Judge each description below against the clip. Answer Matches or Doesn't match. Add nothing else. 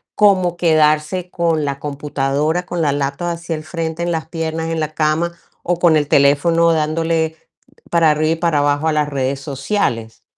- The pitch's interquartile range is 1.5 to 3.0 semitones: Matches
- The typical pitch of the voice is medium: Matches